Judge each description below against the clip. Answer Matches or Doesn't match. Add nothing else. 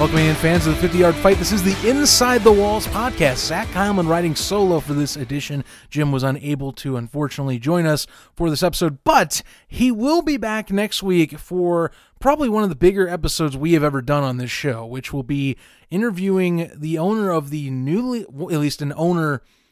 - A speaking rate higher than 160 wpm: Matches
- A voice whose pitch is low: Doesn't match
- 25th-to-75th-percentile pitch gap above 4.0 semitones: Matches